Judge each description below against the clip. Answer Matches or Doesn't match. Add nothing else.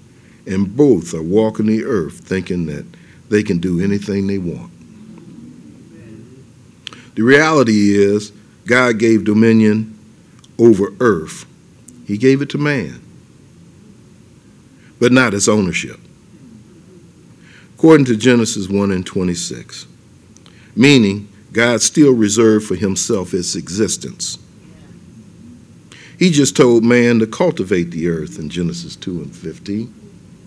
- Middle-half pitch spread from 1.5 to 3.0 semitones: Doesn't match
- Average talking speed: Doesn't match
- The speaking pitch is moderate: Doesn't match